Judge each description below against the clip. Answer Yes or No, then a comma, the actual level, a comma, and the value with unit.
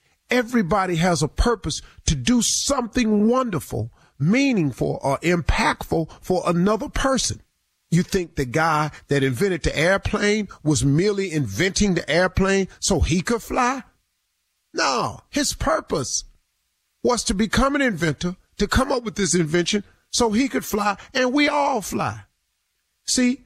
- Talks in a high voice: Yes, high, 195 Hz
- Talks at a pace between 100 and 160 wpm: Yes, average, 140 wpm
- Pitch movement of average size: No, wide, 6.3 semitones